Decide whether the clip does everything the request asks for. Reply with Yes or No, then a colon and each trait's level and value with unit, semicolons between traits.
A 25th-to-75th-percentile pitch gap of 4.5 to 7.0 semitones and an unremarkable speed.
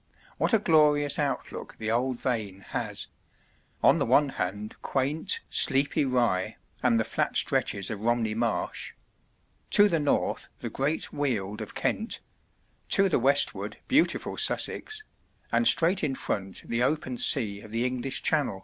Yes: average, 5.3 semitones; average, 150 wpm